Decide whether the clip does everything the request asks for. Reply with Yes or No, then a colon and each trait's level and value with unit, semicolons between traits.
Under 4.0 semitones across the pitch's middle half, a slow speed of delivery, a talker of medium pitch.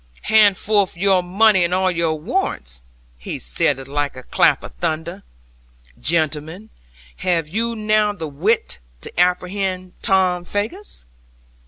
No: average, 4.4 semitones; slow, 130 wpm; medium, 180 Hz